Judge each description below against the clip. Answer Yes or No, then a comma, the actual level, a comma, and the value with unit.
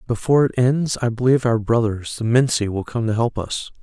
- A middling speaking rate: No, fast, 220 wpm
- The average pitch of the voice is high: No, low, 120 Hz